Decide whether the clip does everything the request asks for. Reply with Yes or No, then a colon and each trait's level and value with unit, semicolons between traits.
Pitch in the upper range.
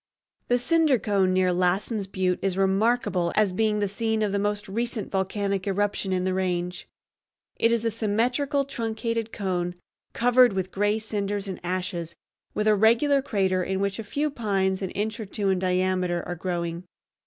Yes: high, 200 Hz